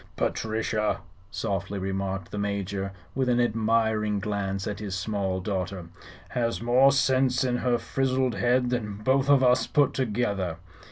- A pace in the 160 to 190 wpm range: No, average, 145 wpm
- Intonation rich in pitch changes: No, average, 4.2 semitones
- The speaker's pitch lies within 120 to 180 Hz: No, low, 110 Hz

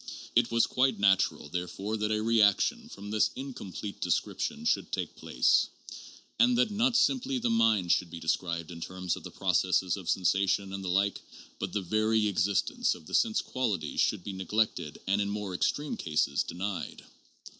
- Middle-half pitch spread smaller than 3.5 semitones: No, average, 3.8 semitones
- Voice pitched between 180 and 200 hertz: No, low, 100 Hz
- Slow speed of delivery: No, average, 175 wpm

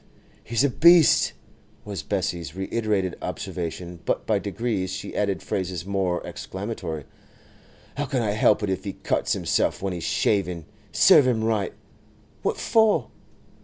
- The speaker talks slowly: Yes, slow, 130 wpm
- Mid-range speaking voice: No, low, 100 Hz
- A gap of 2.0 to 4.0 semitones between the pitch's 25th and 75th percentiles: Yes, average, 3.4 semitones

